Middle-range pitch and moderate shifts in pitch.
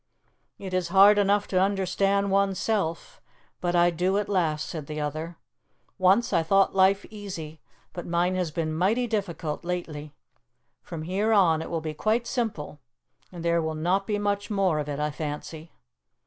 Yes: medium, 180 Hz; average, 3.8 semitones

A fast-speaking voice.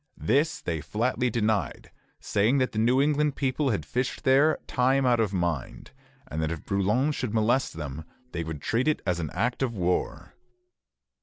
No: average, 175 wpm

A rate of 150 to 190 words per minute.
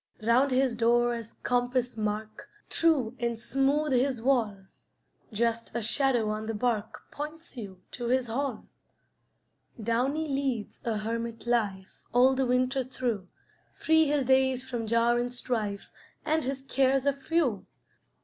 No: average, 140 wpm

